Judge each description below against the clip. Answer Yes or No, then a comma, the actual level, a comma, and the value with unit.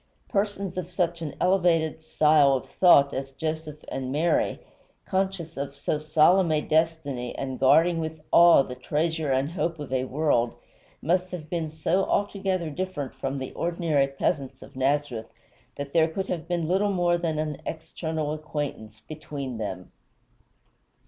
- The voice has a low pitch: No, medium, 155 Hz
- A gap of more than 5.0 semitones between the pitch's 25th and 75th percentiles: No, average, 3.6 semitones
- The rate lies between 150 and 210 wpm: Yes, average, 155 wpm